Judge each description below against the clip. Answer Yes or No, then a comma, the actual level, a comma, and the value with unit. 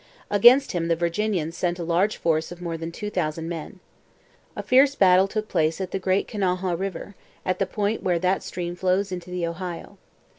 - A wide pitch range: No, narrow, 2.6 semitones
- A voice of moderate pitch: Yes, medium, 180 Hz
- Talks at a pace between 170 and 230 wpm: Yes, average, 195 wpm